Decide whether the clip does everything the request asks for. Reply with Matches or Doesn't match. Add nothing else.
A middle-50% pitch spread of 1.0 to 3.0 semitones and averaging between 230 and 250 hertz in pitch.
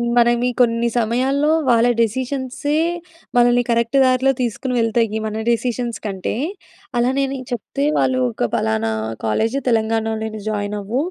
Matches